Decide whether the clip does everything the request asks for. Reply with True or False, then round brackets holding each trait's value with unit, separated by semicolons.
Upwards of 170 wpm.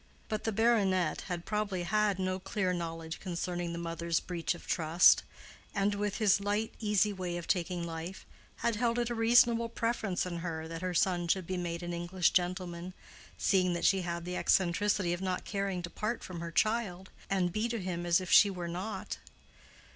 True (190 wpm)